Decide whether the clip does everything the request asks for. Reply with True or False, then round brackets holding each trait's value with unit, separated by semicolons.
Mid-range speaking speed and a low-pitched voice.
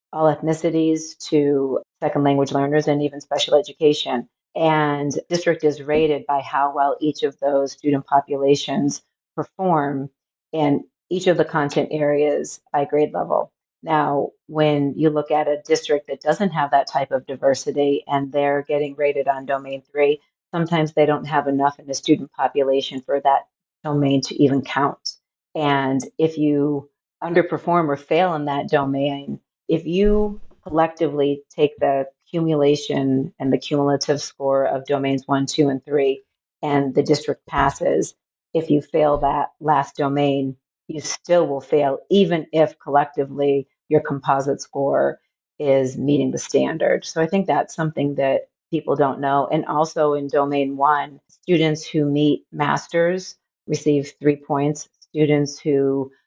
False (150 wpm; 145 Hz)